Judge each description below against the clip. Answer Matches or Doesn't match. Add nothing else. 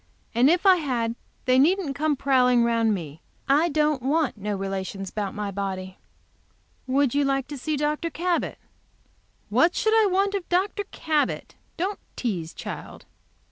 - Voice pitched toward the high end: Matches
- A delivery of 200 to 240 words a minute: Doesn't match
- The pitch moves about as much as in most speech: Doesn't match